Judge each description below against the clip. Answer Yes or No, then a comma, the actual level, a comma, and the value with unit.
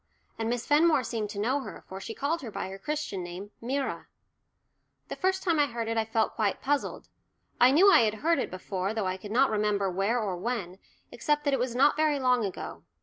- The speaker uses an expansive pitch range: Yes, wide, 5.8 semitones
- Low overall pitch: No, high, 230 Hz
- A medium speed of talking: No, fast, 225 wpm